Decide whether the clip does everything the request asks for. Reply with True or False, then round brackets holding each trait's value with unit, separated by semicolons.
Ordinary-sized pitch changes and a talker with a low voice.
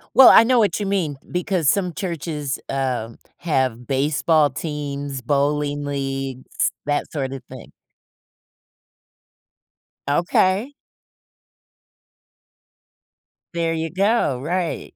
False (4.5 semitones; 150 Hz)